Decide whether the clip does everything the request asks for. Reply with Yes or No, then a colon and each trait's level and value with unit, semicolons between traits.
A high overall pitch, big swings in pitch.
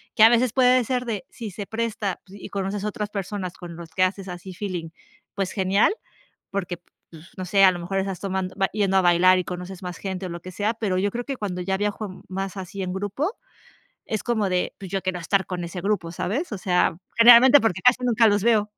No: high, 195 Hz; average, 2.7 semitones